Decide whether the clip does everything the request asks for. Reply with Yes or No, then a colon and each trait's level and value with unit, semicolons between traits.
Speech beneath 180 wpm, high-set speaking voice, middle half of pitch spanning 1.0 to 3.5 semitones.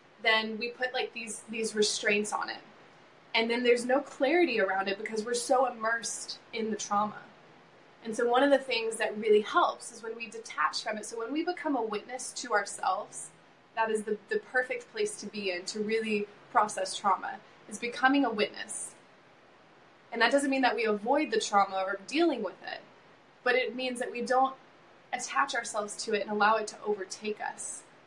No: average, 195 wpm; high, 225 Hz; average, 3.1 semitones